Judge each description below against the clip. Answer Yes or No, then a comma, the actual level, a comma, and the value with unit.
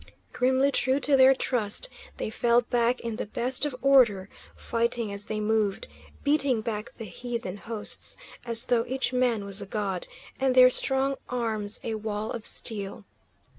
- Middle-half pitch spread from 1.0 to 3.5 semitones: Yes, average, 3.2 semitones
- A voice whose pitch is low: No, high, 235 Hz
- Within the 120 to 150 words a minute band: No, average, 165 wpm